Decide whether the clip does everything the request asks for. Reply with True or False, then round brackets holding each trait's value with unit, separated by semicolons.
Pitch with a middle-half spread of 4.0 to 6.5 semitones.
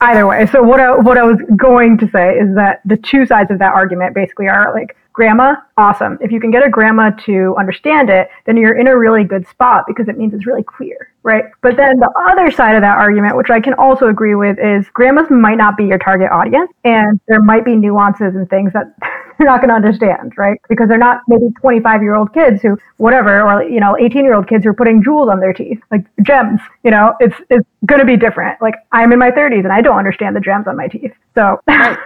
False (3.4 semitones)